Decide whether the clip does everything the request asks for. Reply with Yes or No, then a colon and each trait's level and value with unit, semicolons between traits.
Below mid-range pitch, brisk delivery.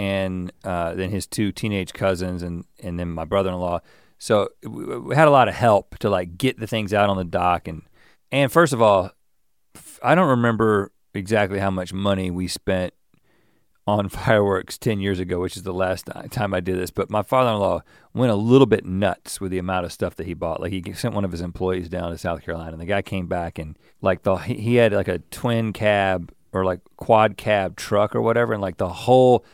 Yes: very low, 95 Hz; fast, 220 wpm